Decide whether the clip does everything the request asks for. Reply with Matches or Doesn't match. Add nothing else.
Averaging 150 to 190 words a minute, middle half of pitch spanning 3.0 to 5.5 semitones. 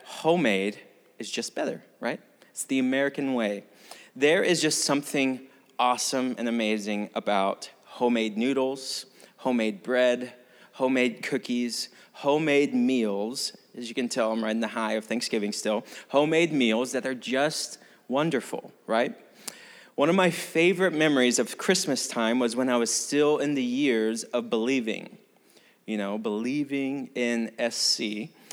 Doesn't match